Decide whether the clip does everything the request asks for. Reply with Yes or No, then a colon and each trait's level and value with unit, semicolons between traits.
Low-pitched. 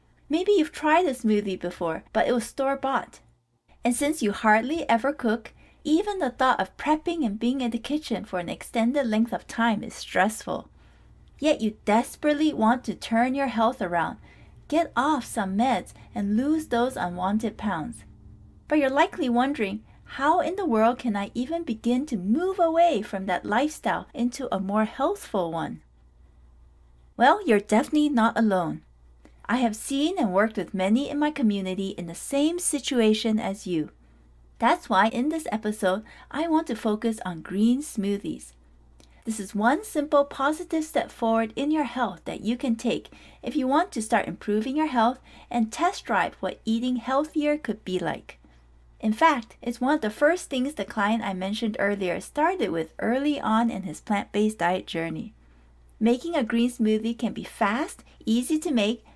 No: high, 230 Hz